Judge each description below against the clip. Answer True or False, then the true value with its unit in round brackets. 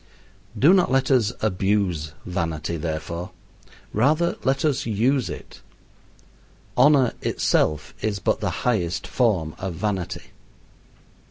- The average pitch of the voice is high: False (105 Hz)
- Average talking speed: False (110 wpm)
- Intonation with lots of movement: True (7.5 semitones)